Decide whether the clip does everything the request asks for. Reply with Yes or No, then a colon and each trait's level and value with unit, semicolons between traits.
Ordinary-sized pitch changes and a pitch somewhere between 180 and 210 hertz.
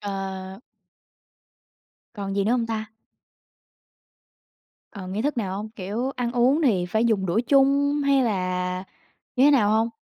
No: average, 4.6 semitones; high, 220 Hz